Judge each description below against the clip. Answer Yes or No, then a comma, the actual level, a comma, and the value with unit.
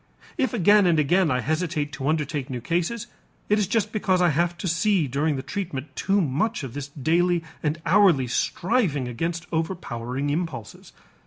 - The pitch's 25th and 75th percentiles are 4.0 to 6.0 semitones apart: Yes, average, 4.6 semitones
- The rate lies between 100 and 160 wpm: No, average, 170 wpm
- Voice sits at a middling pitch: Yes, medium, 165 Hz